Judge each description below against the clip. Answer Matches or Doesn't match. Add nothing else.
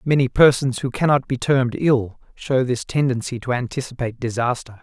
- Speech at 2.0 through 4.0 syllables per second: Doesn't match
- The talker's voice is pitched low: Matches